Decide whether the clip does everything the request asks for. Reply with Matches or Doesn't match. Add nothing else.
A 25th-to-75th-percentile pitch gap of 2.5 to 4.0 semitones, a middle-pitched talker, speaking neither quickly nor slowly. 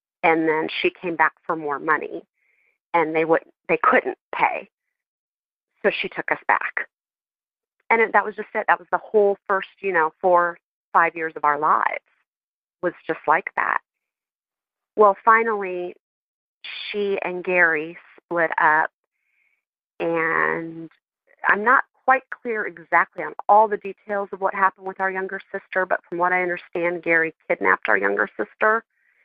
Matches